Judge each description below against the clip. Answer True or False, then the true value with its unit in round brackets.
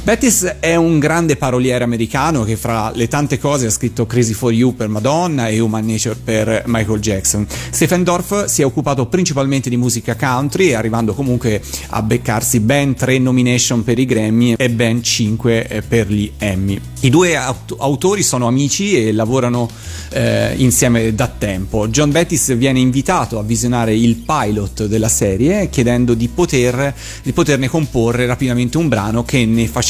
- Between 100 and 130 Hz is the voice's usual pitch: True (120 Hz)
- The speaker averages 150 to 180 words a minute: True (165 wpm)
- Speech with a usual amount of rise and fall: True (3.6 semitones)